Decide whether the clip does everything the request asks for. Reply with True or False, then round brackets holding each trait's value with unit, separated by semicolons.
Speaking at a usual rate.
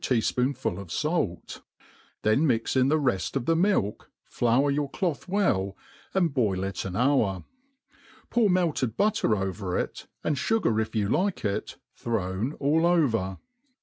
True (150 wpm)